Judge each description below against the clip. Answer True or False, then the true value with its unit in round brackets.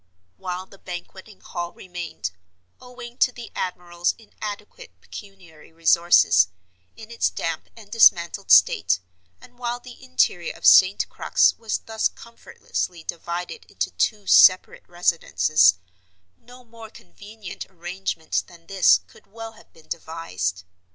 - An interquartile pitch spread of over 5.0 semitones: True (5.6 semitones)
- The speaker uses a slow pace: True (120 wpm)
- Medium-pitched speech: True (180 Hz)